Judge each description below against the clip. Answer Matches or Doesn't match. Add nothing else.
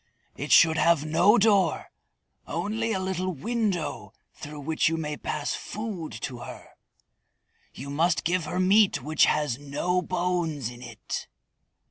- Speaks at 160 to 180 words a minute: Doesn't match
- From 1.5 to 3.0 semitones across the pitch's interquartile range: Doesn't match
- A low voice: Doesn't match